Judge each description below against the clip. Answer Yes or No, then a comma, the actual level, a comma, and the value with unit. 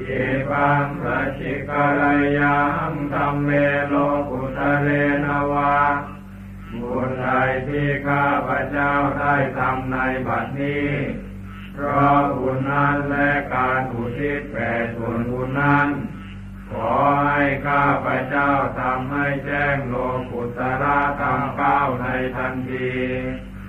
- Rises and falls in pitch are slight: Yes, narrow, 2.0 semitones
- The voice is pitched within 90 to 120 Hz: No, medium, 140 Hz